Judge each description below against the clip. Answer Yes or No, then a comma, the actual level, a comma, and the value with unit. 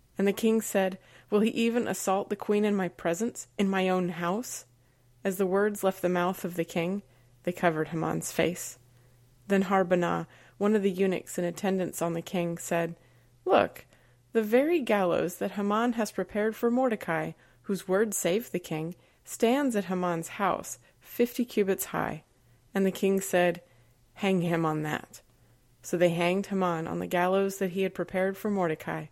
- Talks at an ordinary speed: Yes, average, 175 wpm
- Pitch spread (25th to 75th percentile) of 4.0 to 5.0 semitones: No, average, 3.6 semitones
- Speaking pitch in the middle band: Yes, medium, 180 Hz